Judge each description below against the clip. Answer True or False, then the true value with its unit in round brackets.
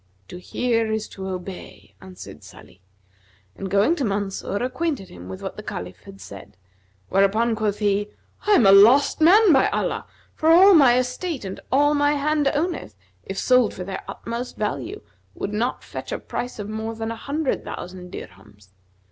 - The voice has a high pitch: True (220 Hz)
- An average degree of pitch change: False (6.6 semitones)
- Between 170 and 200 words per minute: True (175 wpm)